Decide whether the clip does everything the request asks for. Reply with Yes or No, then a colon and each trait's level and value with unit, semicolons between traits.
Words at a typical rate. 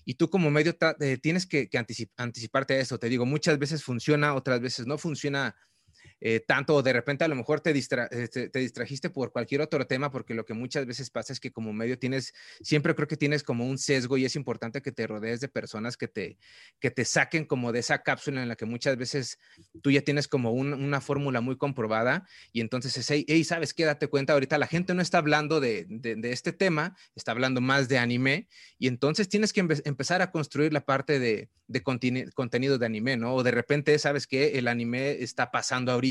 No: fast, 225 wpm